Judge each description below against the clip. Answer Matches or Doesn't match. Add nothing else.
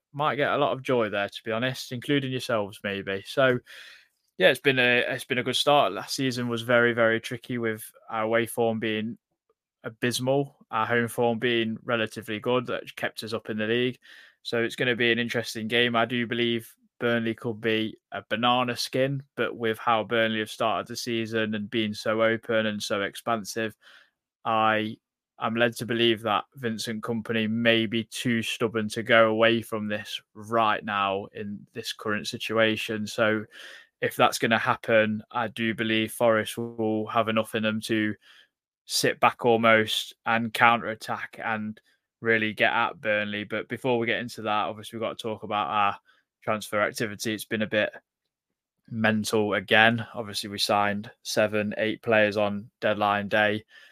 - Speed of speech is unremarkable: Matches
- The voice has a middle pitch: Doesn't match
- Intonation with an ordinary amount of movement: Doesn't match